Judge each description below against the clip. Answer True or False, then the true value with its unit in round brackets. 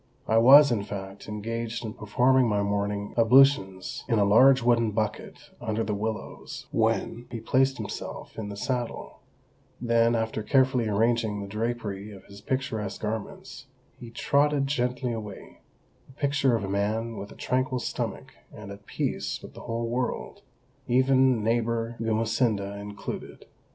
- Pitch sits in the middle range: False (115 Hz)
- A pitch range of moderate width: True (3.2 semitones)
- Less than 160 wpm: True (150 wpm)